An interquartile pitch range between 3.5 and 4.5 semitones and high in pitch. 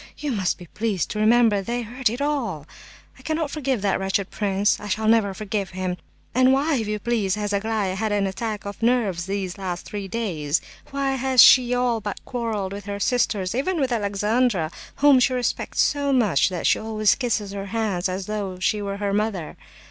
Yes: average, 3.9 semitones; high, 210 Hz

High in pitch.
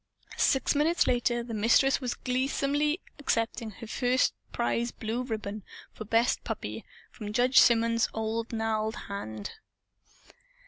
Yes: high, 230 Hz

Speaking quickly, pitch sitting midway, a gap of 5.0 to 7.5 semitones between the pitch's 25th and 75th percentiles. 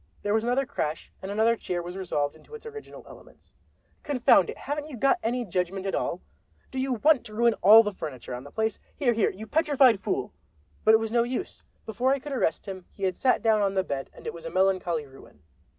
No: fast, 230 wpm; high, 220 Hz; wide, 5.4 semitones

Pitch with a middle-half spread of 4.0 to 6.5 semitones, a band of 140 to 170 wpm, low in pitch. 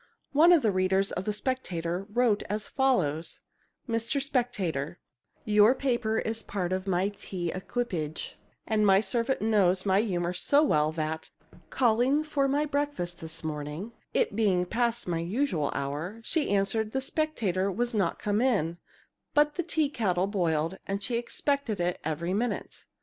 No: wide, 5.6 semitones; average, 160 wpm; high, 205 Hz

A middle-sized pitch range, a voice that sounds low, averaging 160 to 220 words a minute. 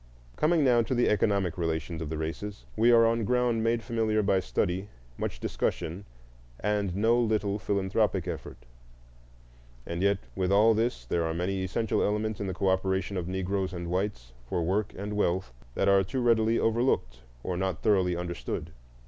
Yes: average, 3.8 semitones; low, 100 Hz; average, 170 wpm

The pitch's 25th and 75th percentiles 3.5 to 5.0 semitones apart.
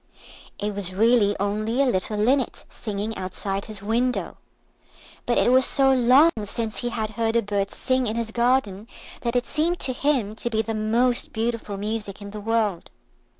No: average, 3.1 semitones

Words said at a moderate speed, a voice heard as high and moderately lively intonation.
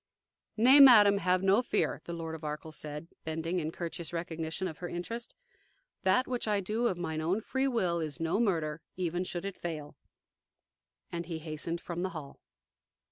No: average, 180 wpm; medium, 175 Hz; average, 3.7 semitones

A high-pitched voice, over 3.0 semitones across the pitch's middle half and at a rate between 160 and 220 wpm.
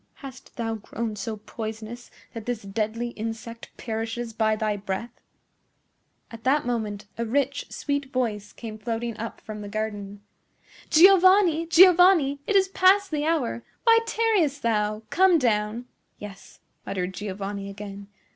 No: high, 230 Hz; average, 5.2 semitones; slow, 135 wpm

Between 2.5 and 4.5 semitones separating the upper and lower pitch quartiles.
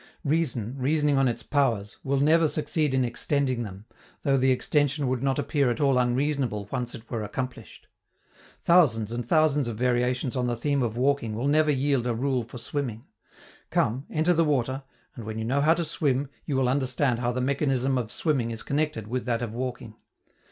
Yes: average, 3.2 semitones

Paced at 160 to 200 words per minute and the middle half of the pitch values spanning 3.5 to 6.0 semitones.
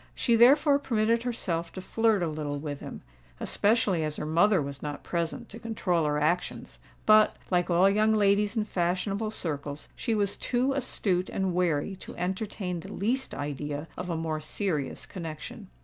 Yes: average, 170 wpm; average, 5.3 semitones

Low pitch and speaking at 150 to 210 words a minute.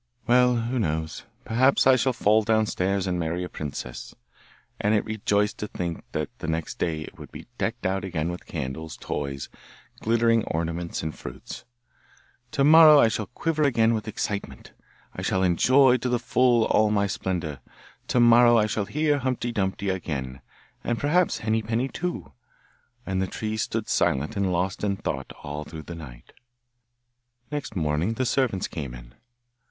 Yes: low, 105 Hz; average, 165 wpm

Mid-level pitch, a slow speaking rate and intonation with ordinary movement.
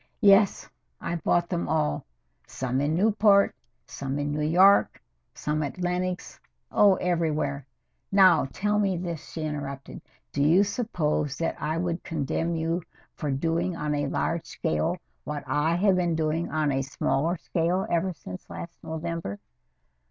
No: medium, 165 Hz; average, 150 wpm; average, 3.3 semitones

